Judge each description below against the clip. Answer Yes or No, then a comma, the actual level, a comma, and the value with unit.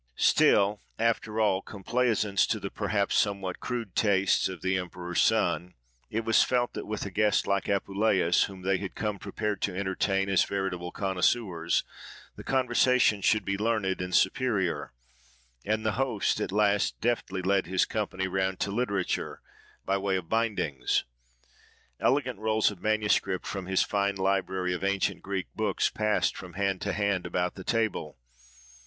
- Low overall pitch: Yes, low, 100 Hz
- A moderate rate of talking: Yes, average, 160 wpm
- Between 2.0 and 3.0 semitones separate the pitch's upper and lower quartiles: Yes, narrow, 2.4 semitones